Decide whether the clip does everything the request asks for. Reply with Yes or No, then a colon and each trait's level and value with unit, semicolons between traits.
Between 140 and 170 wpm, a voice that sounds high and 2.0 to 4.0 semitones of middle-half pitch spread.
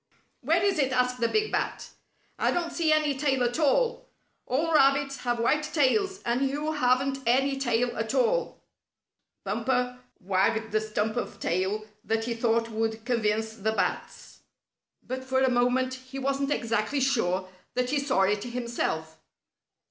Yes: average, 155 wpm; very high, 250 Hz; average, 3.7 semitones